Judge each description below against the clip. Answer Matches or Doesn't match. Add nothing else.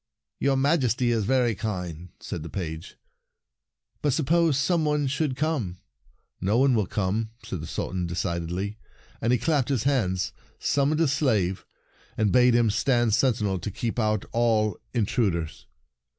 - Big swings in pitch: Matches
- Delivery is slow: Doesn't match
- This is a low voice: Matches